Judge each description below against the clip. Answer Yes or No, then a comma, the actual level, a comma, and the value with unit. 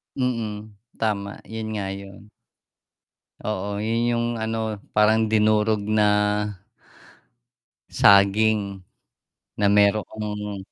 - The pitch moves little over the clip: Yes, narrow, 1.4 semitones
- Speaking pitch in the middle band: No, low, 105 Hz